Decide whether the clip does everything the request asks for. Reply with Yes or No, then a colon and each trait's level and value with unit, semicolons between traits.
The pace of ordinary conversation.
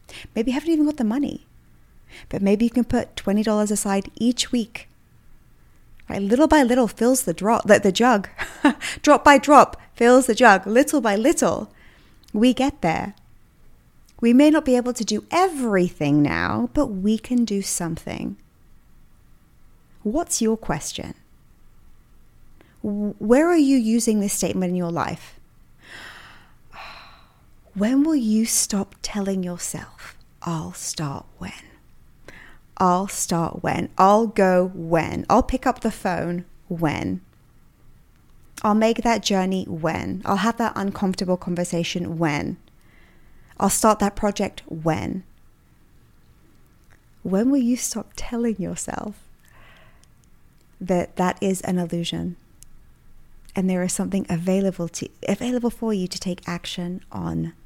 No: slow, 130 wpm